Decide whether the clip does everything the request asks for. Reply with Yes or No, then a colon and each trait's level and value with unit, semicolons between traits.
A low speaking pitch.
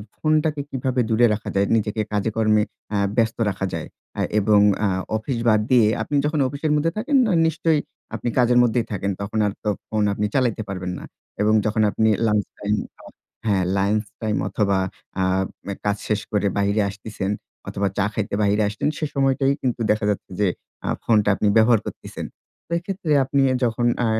Yes: low, 110 Hz